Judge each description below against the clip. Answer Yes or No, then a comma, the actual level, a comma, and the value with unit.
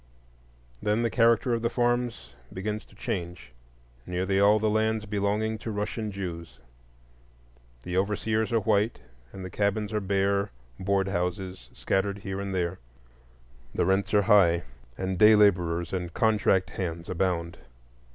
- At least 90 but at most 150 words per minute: Yes, average, 140 wpm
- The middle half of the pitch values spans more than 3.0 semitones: No, narrow, 2.6 semitones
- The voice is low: Yes, low, 100 Hz